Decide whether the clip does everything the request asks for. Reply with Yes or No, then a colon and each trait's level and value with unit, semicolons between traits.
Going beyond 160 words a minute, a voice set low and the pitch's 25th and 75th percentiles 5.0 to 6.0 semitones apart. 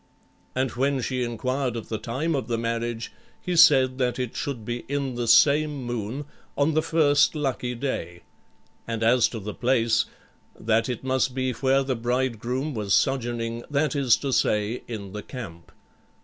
No: average, 170 wpm; low, 125 Hz; average, 2.9 semitones